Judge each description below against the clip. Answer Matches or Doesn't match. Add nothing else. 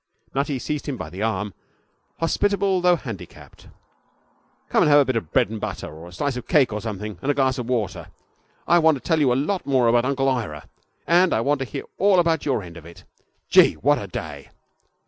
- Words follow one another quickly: Matches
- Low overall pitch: Matches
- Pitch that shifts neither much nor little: Doesn't match